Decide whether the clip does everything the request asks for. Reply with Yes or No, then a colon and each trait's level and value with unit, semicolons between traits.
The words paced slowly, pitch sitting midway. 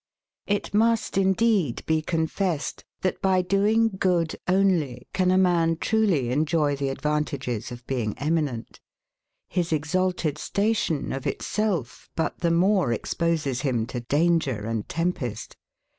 Yes: slow, 130 wpm; medium, 165 Hz